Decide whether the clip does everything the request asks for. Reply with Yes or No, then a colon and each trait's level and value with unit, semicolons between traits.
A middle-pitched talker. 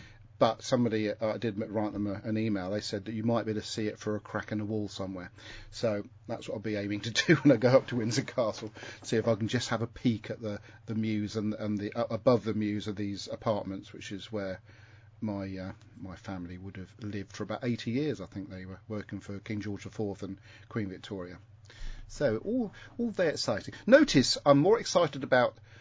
No: low, 110 Hz